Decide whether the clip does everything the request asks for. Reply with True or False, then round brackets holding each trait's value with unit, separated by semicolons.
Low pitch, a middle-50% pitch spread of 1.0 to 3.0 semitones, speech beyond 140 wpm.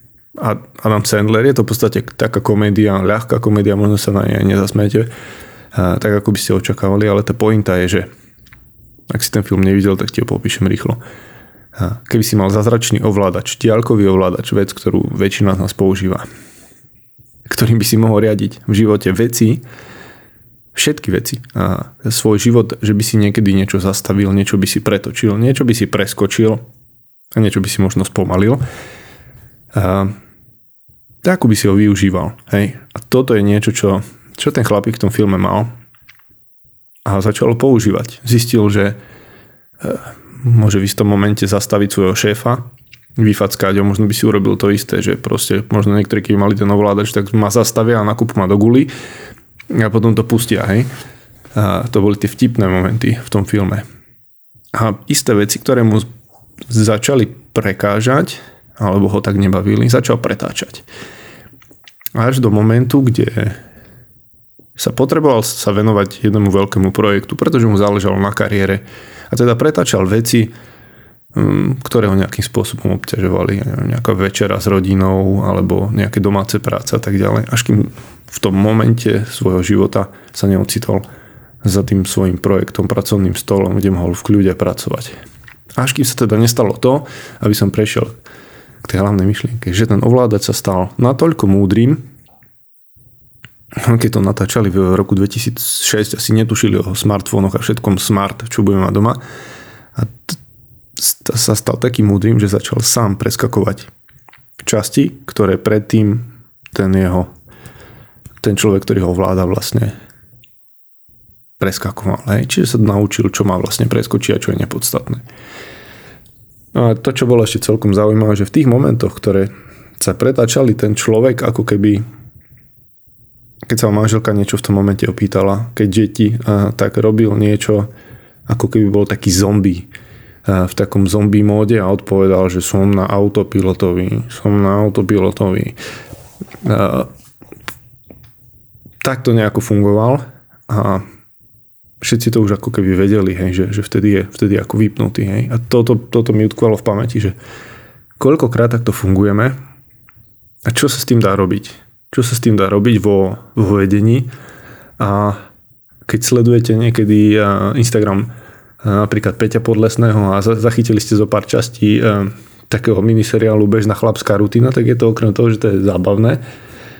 True (105 Hz; 2.7 semitones; 150 wpm)